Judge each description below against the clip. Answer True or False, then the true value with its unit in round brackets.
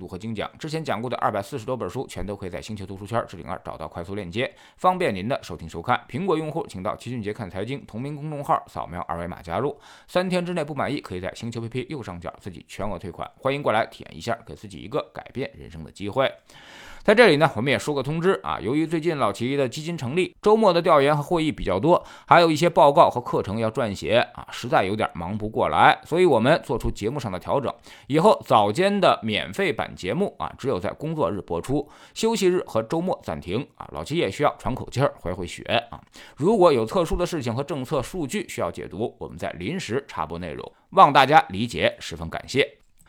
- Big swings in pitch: True (8.4 semitones)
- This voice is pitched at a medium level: False (130 Hz)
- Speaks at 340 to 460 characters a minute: True (350 characters per minute)